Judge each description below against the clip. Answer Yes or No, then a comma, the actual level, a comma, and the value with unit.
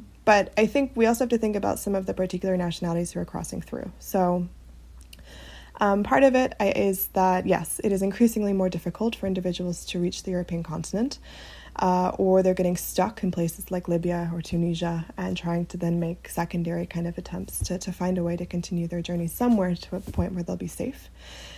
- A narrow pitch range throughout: Yes, narrow, 2.3 semitones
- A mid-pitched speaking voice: Yes, medium, 180 Hz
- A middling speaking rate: No, fast, 210 wpm